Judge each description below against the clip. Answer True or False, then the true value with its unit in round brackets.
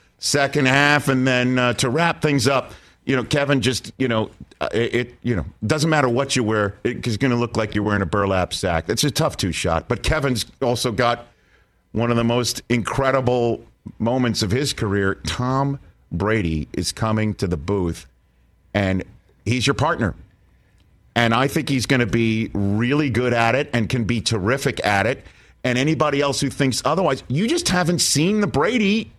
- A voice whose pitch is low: True (120 Hz)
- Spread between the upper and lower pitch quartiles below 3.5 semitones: False (4.1 semitones)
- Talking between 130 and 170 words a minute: False (190 wpm)